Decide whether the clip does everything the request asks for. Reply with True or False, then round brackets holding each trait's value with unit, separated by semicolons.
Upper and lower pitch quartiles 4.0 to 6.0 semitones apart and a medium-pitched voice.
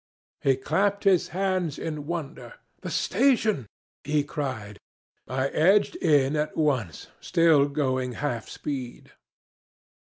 True (4.5 semitones; 150 Hz)